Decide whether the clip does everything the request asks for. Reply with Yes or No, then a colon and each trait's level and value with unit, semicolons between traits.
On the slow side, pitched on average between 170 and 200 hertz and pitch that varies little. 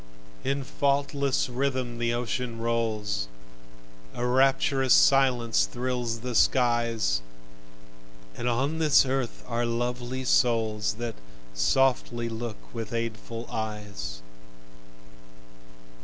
No: slow, 95 wpm; low, 120 Hz; narrow, 2.3 semitones